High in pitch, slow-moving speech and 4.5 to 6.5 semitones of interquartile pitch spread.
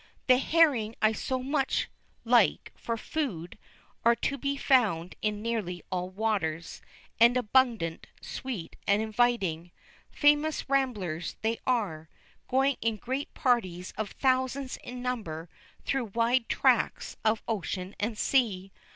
Yes: high, 230 Hz; slow, 125 wpm; average, 5.3 semitones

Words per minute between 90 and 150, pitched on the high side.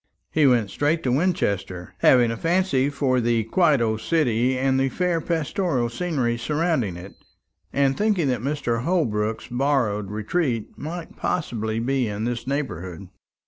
No: average, 145 wpm; low, 130 Hz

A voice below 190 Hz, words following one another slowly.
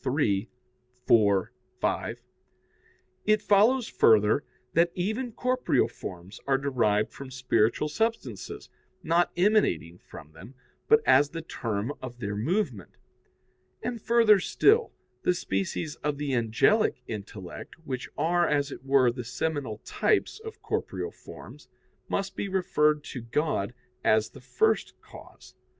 Yes: medium, 140 Hz; slow, 130 wpm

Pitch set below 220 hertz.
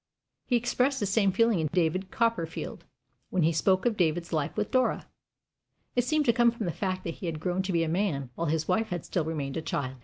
Yes: medium, 185 Hz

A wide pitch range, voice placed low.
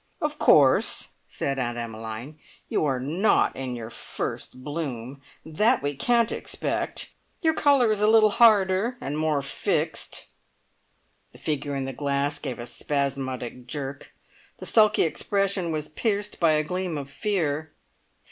No: wide, 6.9 semitones; medium, 150 Hz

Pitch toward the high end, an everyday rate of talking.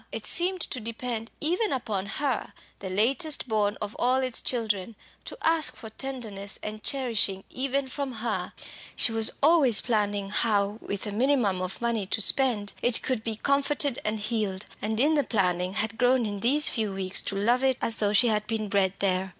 Yes: high, 225 Hz; average, 190 wpm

